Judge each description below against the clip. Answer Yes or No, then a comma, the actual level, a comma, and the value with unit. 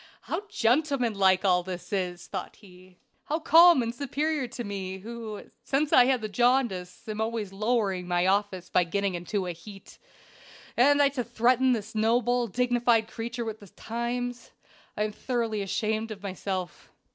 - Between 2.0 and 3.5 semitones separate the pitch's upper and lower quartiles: No, average, 4.1 semitones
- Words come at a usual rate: Yes, average, 165 wpm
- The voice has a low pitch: No, high, 220 Hz